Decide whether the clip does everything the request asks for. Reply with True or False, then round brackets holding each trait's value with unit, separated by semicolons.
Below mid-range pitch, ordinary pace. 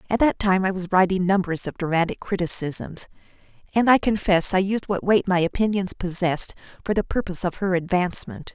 False (190 Hz; 180 wpm)